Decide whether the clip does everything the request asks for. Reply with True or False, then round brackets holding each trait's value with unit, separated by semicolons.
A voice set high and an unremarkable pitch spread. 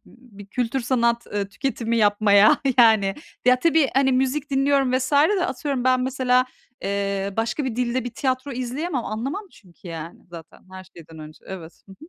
True (245 Hz; 4.9 semitones)